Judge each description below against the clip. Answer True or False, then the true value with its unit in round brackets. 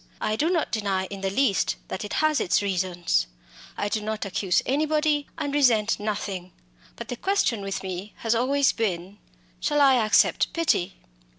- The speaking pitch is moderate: False (215 Hz)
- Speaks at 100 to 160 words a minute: False (170 wpm)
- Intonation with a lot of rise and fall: True (6.4 semitones)